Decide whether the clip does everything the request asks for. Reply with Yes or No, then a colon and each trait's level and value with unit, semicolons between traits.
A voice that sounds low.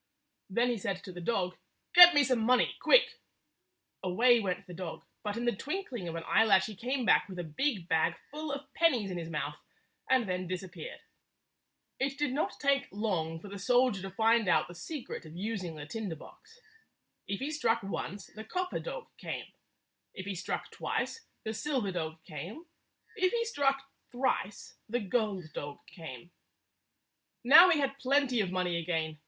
No: high, 215 Hz